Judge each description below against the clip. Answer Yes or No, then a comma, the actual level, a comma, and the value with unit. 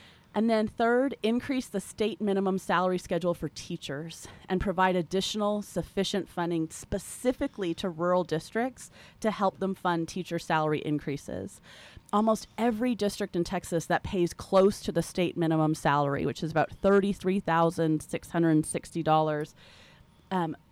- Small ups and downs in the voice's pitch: No, average, 3.8 semitones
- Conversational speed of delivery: No, slow, 130 wpm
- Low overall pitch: No, medium, 180 Hz